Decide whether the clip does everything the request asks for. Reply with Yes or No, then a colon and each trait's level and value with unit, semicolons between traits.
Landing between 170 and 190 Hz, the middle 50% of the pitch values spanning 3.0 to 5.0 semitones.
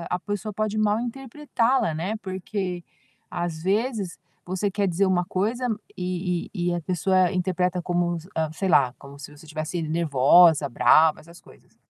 Yes: medium, 185 Hz; average, 4.0 semitones